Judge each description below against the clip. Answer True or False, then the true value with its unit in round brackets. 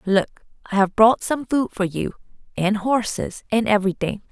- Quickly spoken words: False (165 wpm)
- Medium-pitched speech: False (210 Hz)